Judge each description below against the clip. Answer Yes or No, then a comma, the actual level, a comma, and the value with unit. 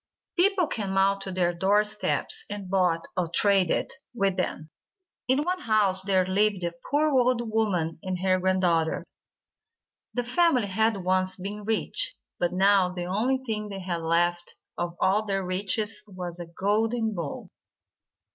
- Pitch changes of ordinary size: Yes, average, 3.2 semitones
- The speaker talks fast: No, average, 155 wpm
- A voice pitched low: No, high, 195 Hz